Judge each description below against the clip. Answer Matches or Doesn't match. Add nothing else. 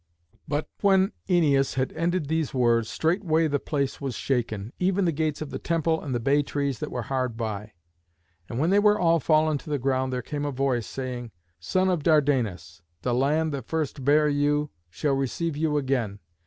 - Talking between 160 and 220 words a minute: Matches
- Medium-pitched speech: Matches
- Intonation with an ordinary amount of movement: Matches